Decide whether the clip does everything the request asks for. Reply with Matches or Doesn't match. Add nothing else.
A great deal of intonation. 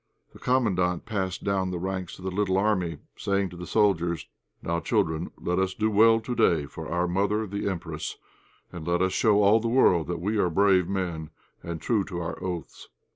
Doesn't match